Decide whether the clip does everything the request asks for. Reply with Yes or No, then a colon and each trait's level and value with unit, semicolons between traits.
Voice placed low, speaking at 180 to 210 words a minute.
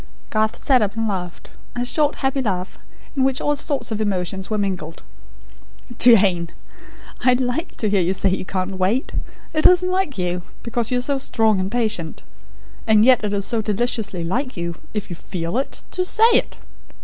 No: high, 215 Hz; average, 185 wpm